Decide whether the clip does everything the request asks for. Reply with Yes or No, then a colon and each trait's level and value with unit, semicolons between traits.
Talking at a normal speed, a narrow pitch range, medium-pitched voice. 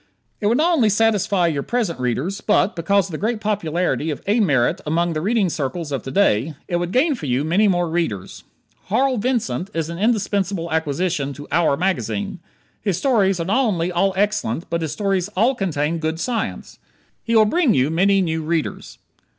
No: average, 190 wpm; average, 4.6 semitones; medium, 180 Hz